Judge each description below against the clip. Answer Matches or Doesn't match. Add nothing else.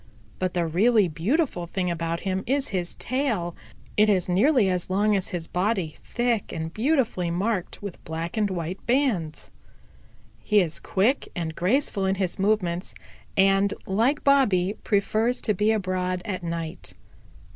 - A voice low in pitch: Doesn't match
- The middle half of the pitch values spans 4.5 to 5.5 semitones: Doesn't match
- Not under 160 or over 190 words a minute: Doesn't match